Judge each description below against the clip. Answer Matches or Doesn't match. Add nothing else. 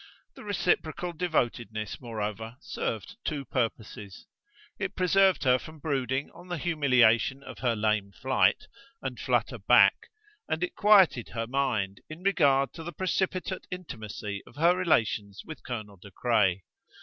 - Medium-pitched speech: Doesn't match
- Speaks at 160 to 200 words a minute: Doesn't match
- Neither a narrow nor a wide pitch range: Doesn't match